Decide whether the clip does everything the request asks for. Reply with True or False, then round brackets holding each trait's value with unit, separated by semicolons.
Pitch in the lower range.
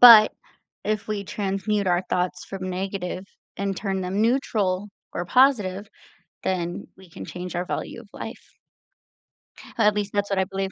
False (195 Hz)